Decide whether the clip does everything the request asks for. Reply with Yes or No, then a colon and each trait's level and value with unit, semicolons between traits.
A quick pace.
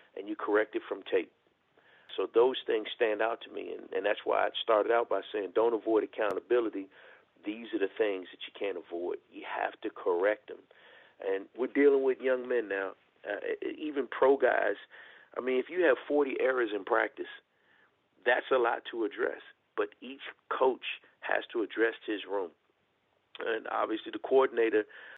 No: average, 180 wpm